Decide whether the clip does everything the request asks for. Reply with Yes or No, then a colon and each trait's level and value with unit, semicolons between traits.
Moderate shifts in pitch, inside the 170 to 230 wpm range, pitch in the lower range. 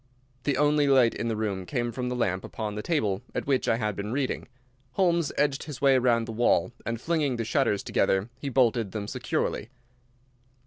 Yes: average, 4.4 semitones; average, 195 wpm; low, 120 Hz